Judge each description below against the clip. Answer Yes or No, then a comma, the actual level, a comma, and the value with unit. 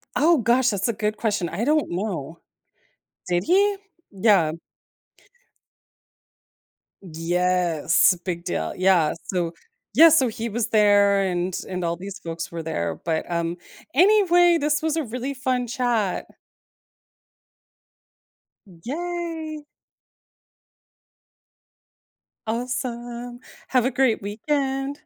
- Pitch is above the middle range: Yes, high, 220 Hz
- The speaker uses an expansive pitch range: Yes, wide, 7.1 semitones